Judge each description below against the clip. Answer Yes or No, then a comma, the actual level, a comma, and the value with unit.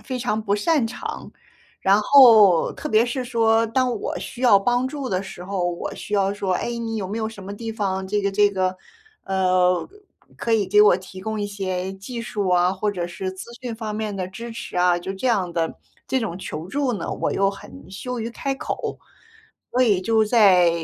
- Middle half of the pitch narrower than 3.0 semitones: No, average, 3.5 semitones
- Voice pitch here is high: Yes, high, 205 Hz